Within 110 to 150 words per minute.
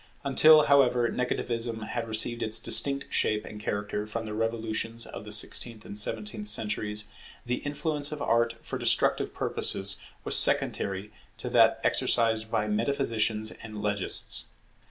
Yes: average, 140 wpm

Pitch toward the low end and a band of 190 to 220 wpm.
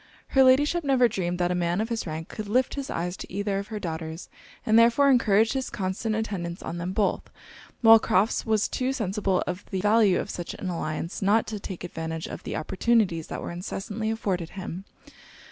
No: high, 200 Hz; average, 200 wpm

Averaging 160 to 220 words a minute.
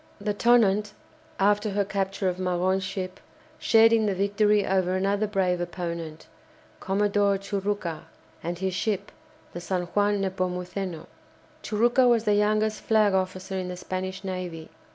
No: average, 140 wpm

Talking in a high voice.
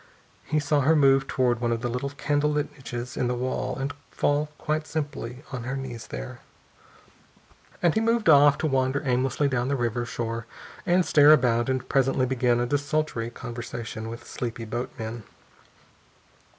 No: low, 130 Hz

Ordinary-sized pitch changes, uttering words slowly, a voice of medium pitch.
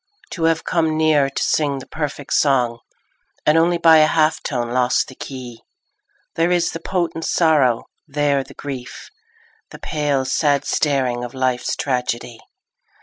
No: average, 3.7 semitones; average, 150 wpm; medium, 145 Hz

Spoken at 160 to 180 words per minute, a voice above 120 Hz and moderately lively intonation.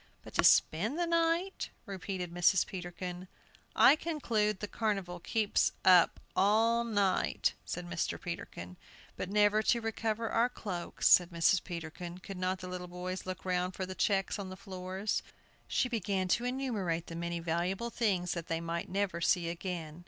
Yes: average, 165 wpm; medium, 185 Hz; average, 3.4 semitones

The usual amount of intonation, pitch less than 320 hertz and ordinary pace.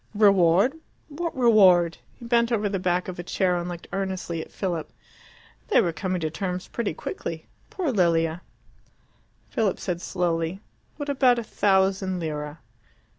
Yes: average, 3.9 semitones; medium, 185 Hz; average, 150 wpm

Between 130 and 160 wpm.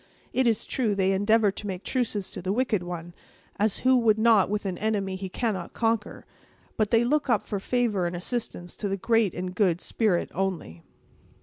No: average, 190 wpm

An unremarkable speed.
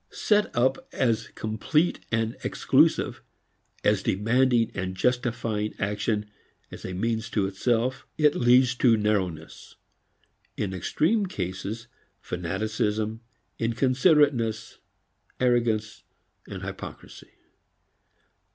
No: slow, 90 wpm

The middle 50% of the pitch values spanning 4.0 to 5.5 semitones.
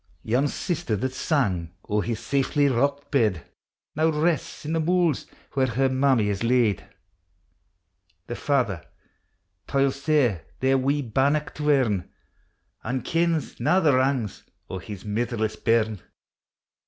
Yes: average, 4.7 semitones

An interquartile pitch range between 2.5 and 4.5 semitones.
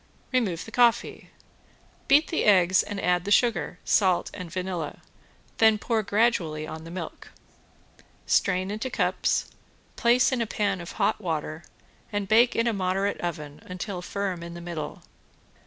Yes: average, 4.2 semitones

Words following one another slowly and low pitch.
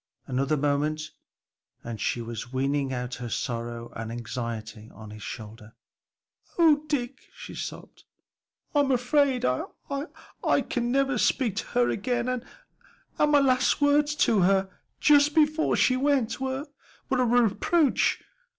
No: slow, 130 wpm; high, 235 Hz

